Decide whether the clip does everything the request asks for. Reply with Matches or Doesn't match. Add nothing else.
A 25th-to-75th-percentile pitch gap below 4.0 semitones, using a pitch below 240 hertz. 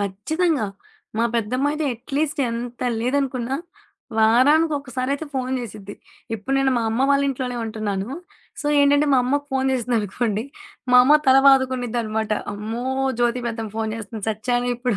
Doesn't match